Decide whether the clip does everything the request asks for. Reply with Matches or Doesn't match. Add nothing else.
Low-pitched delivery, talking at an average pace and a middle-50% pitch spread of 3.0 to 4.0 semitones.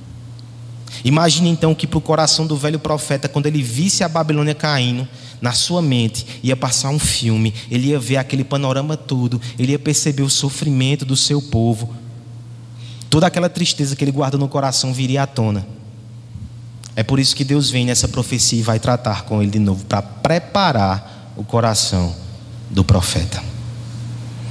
Matches